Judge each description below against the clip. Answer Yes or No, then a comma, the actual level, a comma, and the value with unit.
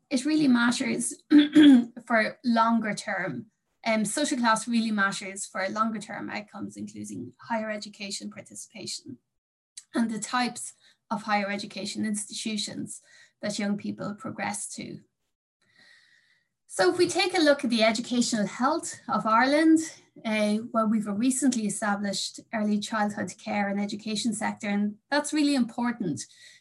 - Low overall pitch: No, high, 225 Hz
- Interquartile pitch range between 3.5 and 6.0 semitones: Yes, average, 4.1 semitones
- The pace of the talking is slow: Yes, slow, 130 wpm